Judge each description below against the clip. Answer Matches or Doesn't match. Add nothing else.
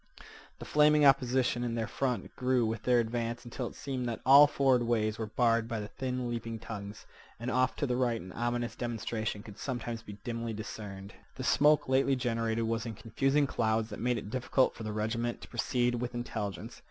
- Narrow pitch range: Matches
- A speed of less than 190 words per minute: Doesn't match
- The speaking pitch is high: Doesn't match